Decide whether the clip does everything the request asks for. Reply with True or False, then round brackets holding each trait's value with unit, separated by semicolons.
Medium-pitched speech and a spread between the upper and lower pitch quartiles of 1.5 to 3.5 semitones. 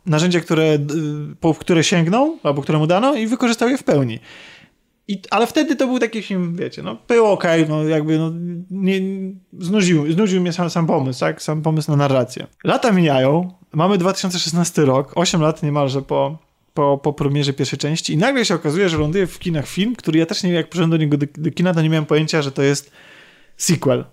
False (165 Hz; 3.9 semitones)